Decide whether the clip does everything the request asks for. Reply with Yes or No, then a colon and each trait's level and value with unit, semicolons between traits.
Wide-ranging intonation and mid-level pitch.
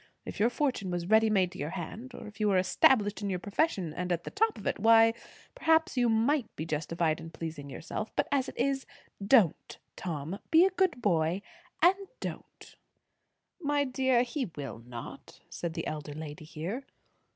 No: wide, 7.9 semitones; high, 205 Hz